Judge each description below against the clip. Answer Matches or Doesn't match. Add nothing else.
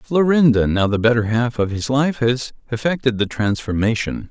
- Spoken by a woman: Doesn't match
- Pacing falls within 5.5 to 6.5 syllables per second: Doesn't match